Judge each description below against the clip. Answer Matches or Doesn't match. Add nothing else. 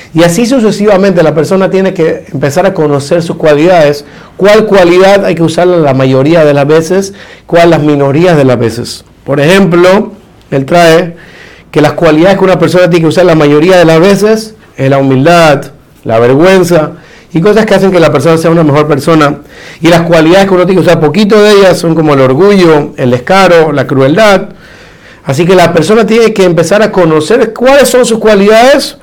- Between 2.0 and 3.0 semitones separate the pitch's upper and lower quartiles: Doesn't match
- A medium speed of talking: Doesn't match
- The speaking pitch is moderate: Matches